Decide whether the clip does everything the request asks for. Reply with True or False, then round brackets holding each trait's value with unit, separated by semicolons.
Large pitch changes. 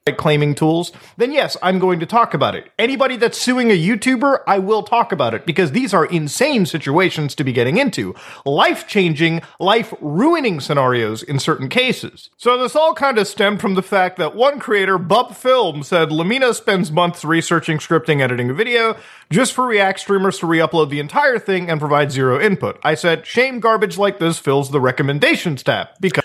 True (6.1 semitones)